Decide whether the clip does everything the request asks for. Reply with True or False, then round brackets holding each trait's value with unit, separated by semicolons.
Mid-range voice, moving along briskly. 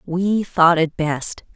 False (170 Hz; 155 wpm)